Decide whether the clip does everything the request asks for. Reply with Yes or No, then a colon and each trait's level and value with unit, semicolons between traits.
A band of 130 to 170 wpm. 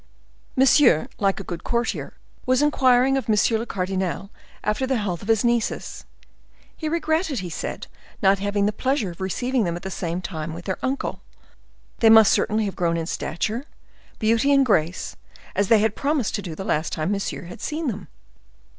No: average, 185 wpm